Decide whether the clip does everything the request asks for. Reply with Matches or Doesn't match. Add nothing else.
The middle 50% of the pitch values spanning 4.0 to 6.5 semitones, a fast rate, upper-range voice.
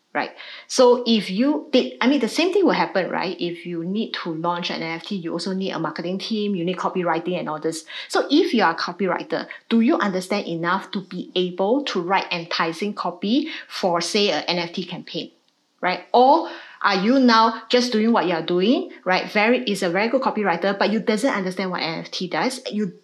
Matches